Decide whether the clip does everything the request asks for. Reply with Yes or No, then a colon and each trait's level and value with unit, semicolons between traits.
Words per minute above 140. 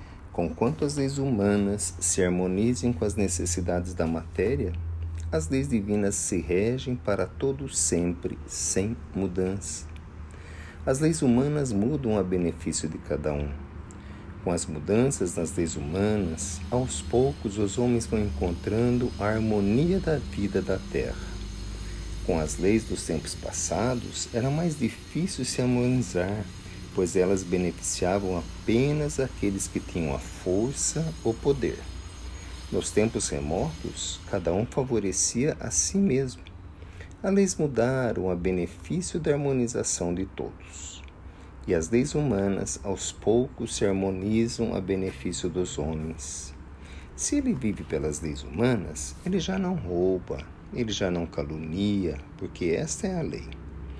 No: average, 130 wpm